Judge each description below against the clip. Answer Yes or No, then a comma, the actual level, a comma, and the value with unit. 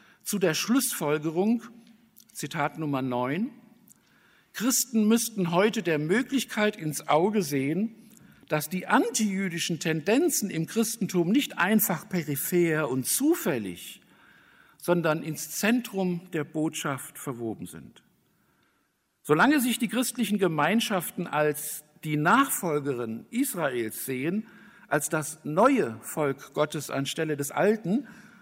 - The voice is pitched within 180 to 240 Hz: Yes, medium, 185 Hz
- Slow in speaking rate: Yes, slow, 105 wpm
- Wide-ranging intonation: Yes, wide, 6.9 semitones